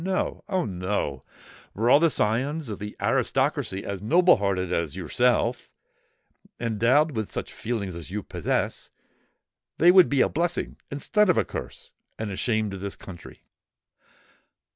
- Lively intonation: Yes, wide, 7.6 semitones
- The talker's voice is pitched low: Yes, low, 110 Hz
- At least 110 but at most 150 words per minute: Yes, average, 140 wpm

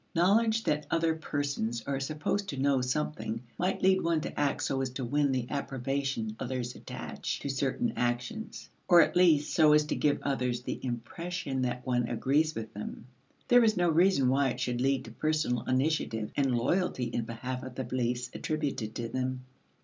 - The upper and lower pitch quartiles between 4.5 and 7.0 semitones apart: No, average, 4.0 semitones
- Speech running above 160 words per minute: Yes, average, 185 wpm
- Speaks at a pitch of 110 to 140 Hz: Yes, low, 135 Hz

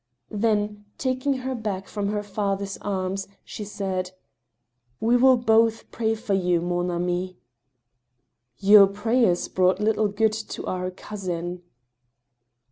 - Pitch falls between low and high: No, high, 200 Hz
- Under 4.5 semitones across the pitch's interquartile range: Yes, average, 3.3 semitones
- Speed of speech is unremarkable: No, slow, 130 wpm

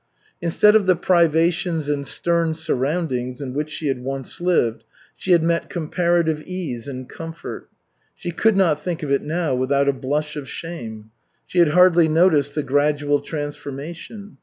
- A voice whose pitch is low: No, medium, 155 Hz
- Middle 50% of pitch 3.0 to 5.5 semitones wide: Yes, average, 3.6 semitones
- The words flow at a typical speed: Yes, average, 160 wpm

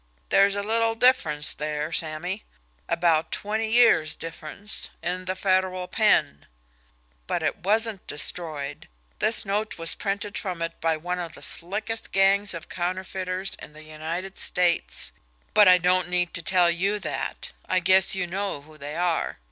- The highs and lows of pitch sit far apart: No, average, 3.3 semitones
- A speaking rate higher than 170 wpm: No, average, 155 wpm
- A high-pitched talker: No, medium, 180 Hz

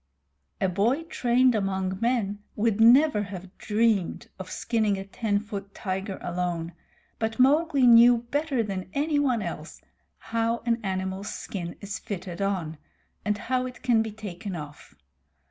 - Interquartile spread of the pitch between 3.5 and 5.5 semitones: Yes, average, 3.9 semitones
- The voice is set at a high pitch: Yes, high, 210 Hz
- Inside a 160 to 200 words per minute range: No, average, 145 wpm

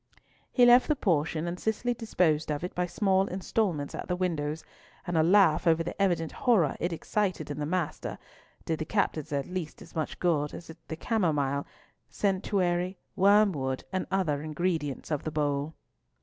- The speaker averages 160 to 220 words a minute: Yes, average, 170 wpm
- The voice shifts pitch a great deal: No, average, 3.9 semitones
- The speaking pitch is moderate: Yes, medium, 175 Hz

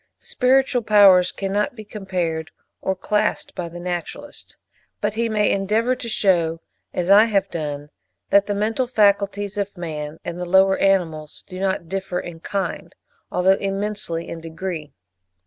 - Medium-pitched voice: No, high, 195 Hz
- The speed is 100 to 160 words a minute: Yes, average, 150 wpm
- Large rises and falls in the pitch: No, average, 3.2 semitones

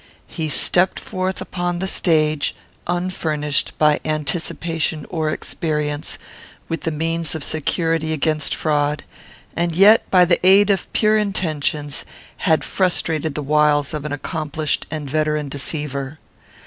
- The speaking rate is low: Yes, slow, 130 wpm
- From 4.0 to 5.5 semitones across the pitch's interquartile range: No, narrow, 2.6 semitones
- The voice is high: No, medium, 155 Hz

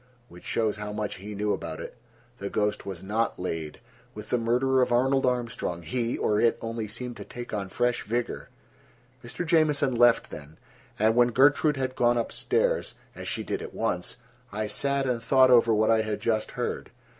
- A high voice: No, low, 115 Hz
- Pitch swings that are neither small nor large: Yes, average, 3.1 semitones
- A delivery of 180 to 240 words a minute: Yes, average, 190 wpm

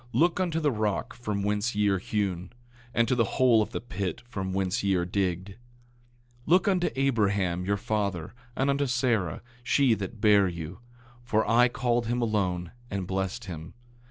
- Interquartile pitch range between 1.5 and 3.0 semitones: No, average, 4.2 semitones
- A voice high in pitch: No, low, 105 Hz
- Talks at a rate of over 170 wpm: Yes, average, 180 wpm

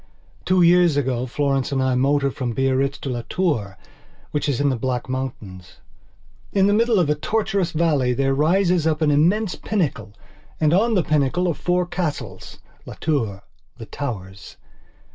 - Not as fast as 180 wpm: Yes, average, 160 wpm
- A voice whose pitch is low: No, medium, 145 Hz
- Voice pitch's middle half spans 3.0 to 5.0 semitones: No, wide, 5.6 semitones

